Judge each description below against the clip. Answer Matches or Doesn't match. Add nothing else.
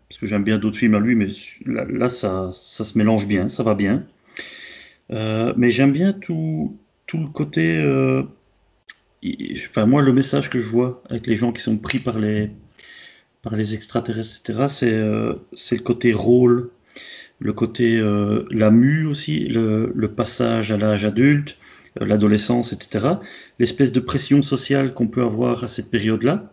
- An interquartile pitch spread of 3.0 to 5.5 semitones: Matches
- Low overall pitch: Matches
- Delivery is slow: Doesn't match